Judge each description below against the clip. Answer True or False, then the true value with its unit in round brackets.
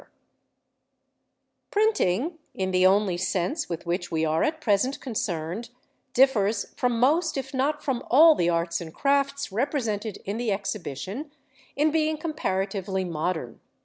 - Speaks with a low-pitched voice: False (215 Hz)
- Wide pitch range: True (7.4 semitones)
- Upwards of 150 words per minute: False (140 wpm)